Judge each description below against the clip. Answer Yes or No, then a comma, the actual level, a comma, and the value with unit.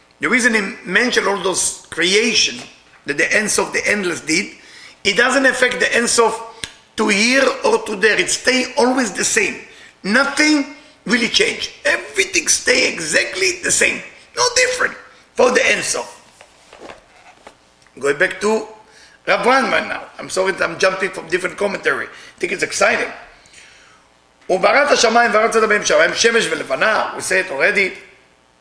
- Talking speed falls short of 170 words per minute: Yes, average, 140 wpm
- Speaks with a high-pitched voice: Yes, high, 230 Hz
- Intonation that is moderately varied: No, wide, 5.7 semitones